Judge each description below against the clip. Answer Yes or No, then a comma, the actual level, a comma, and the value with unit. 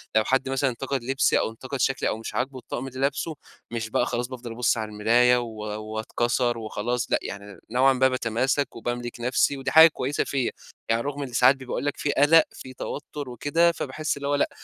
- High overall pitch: No, low, 125 Hz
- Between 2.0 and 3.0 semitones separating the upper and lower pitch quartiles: Yes, average, 2.7 semitones